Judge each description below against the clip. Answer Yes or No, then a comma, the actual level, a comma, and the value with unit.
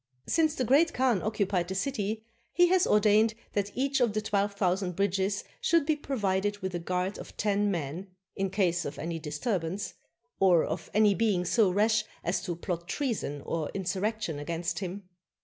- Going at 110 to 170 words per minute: No, average, 180 wpm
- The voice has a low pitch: No, high, 200 Hz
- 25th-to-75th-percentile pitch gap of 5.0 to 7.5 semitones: No, average, 3.5 semitones